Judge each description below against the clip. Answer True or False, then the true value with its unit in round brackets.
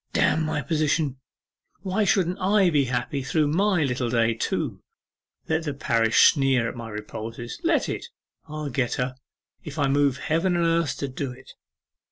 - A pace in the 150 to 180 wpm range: True (170 wpm)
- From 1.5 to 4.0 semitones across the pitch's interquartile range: False (4.7 semitones)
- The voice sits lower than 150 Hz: True (140 Hz)